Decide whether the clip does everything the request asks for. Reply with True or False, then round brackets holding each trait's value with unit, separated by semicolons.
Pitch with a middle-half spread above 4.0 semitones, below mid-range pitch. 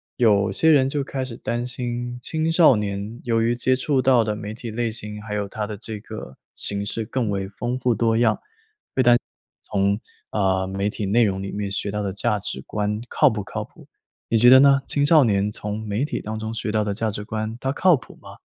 False (3.1 semitones; 110 Hz)